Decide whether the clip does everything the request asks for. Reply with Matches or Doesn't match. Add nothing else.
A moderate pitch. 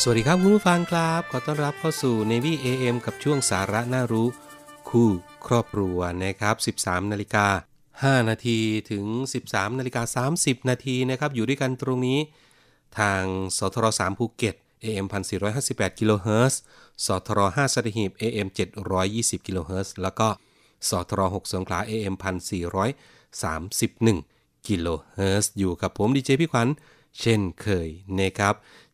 Doesn't match